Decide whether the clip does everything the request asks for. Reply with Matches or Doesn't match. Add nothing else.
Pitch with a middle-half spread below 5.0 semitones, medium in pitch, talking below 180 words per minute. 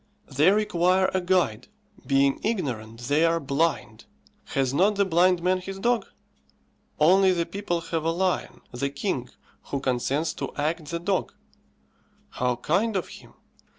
Doesn't match